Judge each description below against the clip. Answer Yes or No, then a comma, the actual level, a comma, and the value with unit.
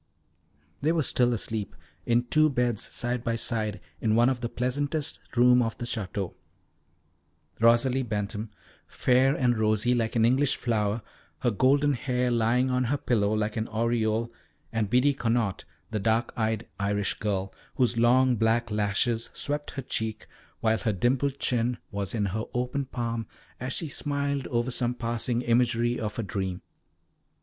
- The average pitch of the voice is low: Yes, low, 120 Hz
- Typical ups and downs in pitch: No, narrow, 2.3 semitones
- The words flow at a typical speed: Yes, average, 160 wpm